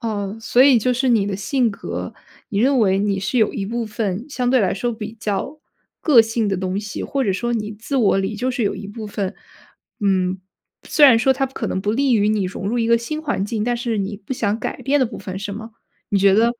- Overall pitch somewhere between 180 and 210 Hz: No, high, 220 Hz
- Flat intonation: No, average, 3.5 semitones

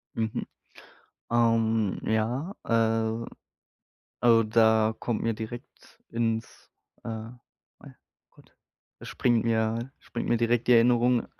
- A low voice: Yes, low, 115 Hz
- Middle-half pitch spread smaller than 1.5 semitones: Yes, narrow, 1.1 semitones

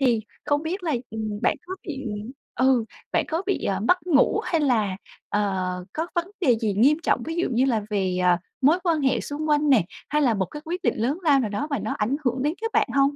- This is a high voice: Yes, very high, 270 Hz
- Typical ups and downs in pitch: No, wide, 6.3 semitones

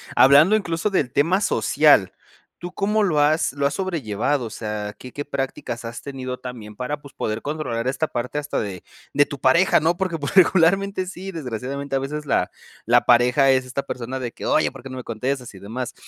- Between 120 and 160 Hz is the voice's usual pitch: Yes, medium, 140 Hz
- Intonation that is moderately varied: Yes, average, 4.6 semitones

